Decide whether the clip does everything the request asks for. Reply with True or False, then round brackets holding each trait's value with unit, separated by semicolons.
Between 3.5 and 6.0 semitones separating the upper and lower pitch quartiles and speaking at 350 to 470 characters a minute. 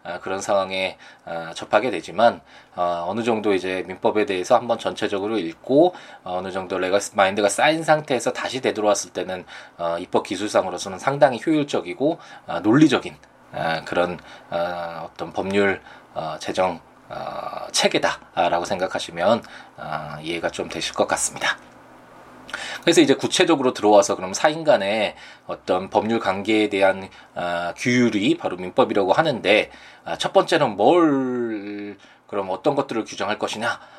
False (5.5 semitones; 295 characters per minute)